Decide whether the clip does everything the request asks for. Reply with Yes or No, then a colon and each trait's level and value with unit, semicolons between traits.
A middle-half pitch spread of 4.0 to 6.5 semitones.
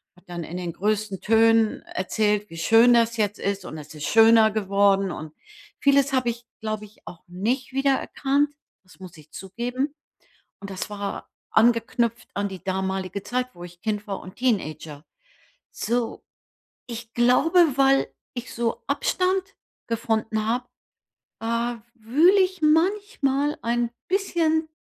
Yes: average, 4.6 semitones